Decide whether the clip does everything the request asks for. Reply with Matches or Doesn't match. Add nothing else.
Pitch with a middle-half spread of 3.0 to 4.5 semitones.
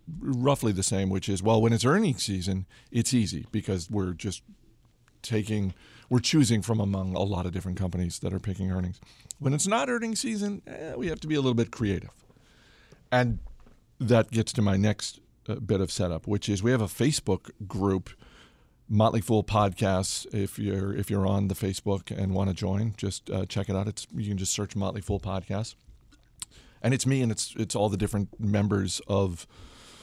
Matches